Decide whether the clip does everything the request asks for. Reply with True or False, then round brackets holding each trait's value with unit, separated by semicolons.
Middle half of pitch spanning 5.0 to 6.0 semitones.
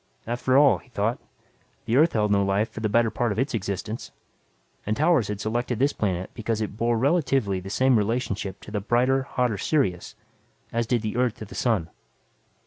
False (3.5 semitones)